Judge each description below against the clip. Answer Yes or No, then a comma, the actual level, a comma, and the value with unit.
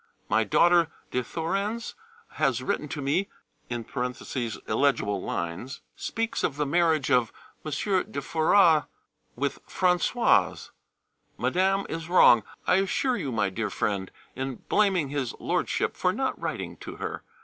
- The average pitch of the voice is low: No, medium, 150 Hz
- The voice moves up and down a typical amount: No, wide, 6.3 semitones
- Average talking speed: No, slow, 130 wpm